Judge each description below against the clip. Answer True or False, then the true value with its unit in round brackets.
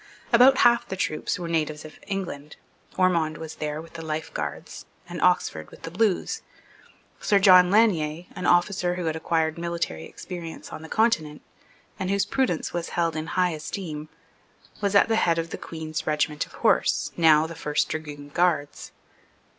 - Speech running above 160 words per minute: True (170 wpm)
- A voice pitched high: False (165 Hz)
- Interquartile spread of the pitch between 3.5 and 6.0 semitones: False (2.9 semitones)